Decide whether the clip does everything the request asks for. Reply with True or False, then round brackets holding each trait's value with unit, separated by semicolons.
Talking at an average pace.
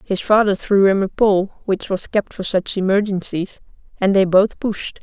True (190 wpm)